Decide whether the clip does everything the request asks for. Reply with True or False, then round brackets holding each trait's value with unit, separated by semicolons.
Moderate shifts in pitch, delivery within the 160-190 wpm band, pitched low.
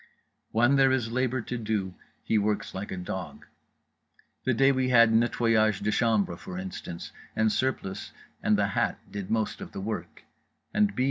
True (3.7 semitones; 175 wpm; 110 Hz)